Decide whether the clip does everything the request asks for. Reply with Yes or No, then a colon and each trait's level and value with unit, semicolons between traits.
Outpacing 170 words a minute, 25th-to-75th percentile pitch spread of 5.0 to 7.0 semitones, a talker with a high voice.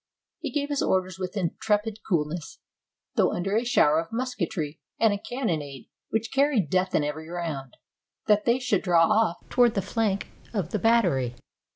Yes: average, 180 wpm; average, 5.3 semitones; high, 195 Hz